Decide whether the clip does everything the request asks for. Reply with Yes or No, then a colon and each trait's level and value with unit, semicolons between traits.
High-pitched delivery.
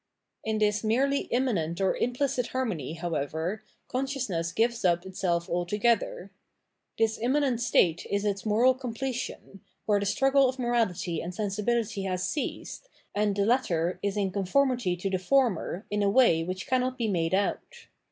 Yes: high, 210 Hz